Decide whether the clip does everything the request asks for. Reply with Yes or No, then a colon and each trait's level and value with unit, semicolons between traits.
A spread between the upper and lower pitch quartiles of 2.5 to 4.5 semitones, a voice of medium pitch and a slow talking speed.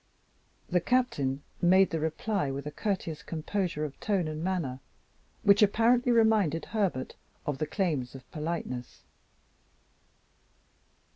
No: wide, 5.5 semitones; medium, 170 Hz; slow, 120 wpm